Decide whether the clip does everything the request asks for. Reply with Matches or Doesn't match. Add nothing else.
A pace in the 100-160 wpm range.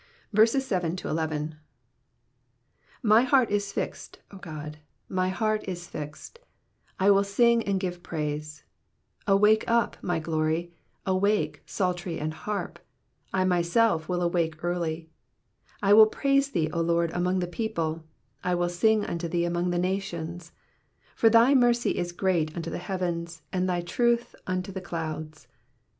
Matches